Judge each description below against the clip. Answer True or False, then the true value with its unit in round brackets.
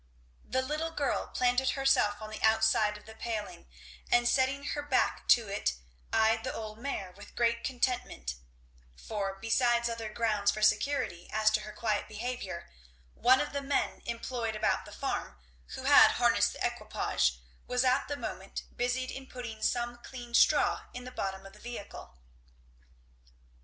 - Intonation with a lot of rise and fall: False (3.0 semitones)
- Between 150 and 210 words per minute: True (165 wpm)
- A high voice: True (230 Hz)